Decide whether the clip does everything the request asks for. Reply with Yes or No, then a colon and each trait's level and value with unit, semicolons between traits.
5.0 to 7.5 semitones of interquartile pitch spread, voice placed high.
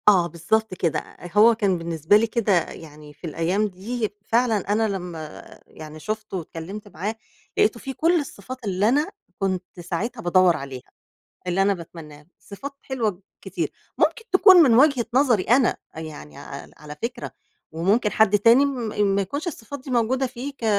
Yes: wide, 5.6 semitones; high, 205 Hz